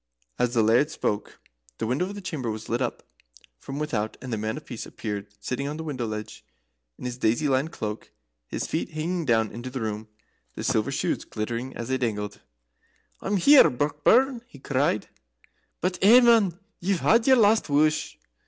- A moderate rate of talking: Yes, average, 185 wpm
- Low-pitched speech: Yes, low, 130 Hz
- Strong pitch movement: Yes, wide, 6.9 semitones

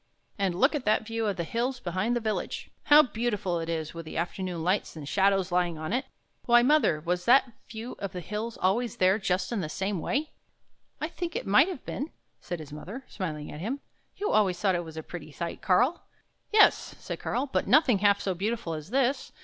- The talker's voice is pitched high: Yes, high, 200 Hz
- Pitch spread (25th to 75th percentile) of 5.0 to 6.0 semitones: Yes, wide, 5.6 semitones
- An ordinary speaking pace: No, fast, 230 wpm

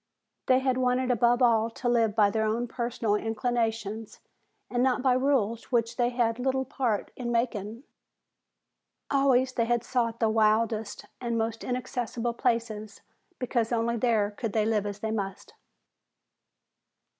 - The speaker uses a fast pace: No, average, 145 wpm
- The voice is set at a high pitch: Yes, high, 235 Hz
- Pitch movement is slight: Yes, narrow, 2.0 semitones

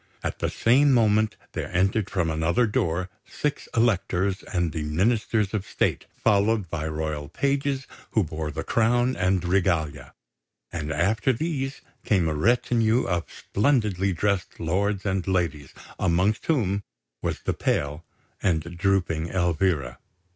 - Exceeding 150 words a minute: No, slow, 135 wpm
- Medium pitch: No, very low, 95 Hz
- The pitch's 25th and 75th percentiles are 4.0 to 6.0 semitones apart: Yes, average, 5.1 semitones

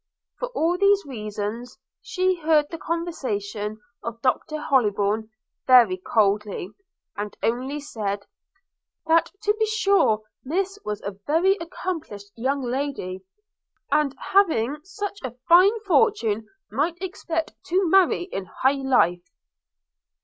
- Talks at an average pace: No, slow, 120 wpm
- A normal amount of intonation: No, wide, 8.7 semitones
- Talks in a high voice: Yes, very high, 275 Hz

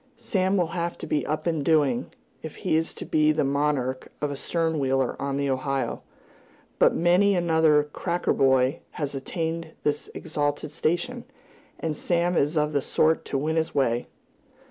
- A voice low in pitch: No, medium, 155 Hz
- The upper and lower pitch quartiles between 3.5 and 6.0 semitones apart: No, average, 3.1 semitones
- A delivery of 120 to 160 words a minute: No, average, 170 wpm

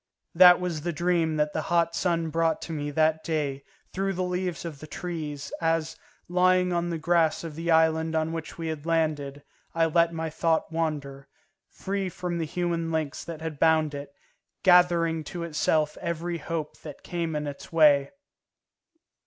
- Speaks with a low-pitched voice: No, medium, 165 Hz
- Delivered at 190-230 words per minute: No, average, 175 wpm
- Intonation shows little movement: Yes, narrow, 1.8 semitones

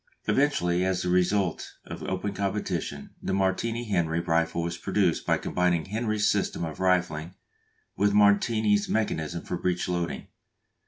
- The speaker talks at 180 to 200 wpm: No, average, 140 wpm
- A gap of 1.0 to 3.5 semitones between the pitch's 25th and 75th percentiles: Yes, average, 3.1 semitones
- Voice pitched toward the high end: No, very low, 90 Hz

